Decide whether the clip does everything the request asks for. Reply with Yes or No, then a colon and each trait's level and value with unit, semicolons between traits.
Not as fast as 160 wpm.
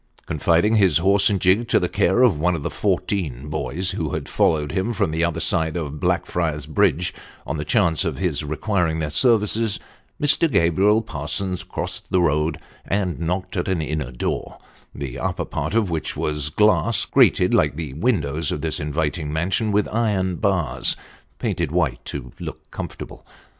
No: average, 175 wpm